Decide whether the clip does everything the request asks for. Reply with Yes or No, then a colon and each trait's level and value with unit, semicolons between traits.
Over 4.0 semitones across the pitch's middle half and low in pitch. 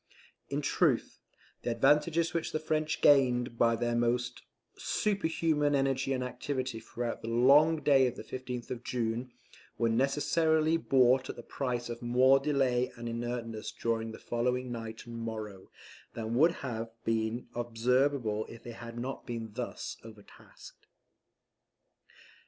No: average, 2.8 semitones; low, 125 Hz